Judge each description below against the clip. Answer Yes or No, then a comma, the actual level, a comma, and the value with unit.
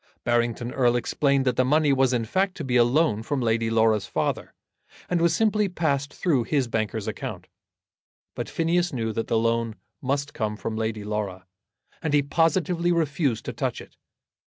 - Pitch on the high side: No, low, 130 Hz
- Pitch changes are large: Yes, wide, 5.7 semitones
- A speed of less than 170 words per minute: No, average, 180 wpm